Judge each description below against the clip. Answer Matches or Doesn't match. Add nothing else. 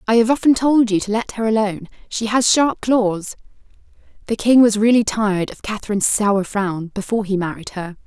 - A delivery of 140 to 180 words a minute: Doesn't match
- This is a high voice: Matches